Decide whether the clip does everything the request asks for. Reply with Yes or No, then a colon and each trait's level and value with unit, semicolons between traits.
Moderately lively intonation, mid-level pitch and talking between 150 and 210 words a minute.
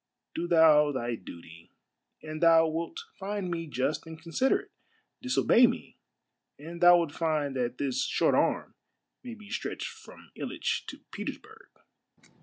No: average, 4.8 semitones; medium, 165 Hz; average, 140 wpm